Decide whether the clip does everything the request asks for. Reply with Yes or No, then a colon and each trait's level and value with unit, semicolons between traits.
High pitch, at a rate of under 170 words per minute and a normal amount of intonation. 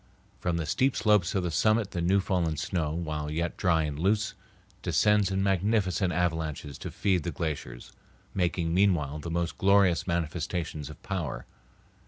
No: very low, 85 Hz; average, 160 wpm; average, 3.6 semitones